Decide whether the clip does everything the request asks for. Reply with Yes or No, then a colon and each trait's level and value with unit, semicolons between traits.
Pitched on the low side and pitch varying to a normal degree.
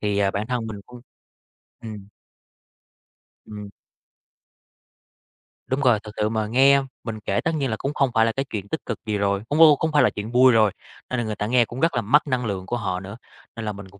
Yes: low, 110 Hz; average, 3.7 semitones